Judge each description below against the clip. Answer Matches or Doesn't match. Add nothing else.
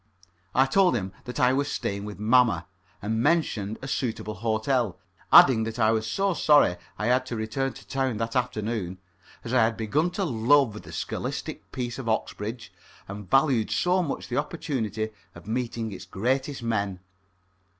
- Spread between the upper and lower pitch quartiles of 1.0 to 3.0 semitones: Doesn't match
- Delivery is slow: Doesn't match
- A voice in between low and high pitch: Doesn't match